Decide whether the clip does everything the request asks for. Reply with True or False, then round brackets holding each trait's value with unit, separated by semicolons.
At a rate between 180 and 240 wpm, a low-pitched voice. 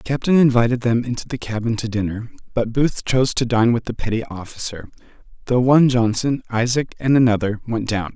True (190 wpm; 120 Hz)